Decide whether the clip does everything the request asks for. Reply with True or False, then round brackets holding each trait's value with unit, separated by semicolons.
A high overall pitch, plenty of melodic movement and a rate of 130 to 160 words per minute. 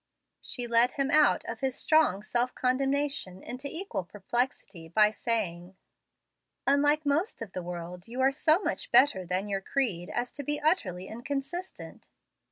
True (245 Hz; 6.9 semitones; 155 wpm)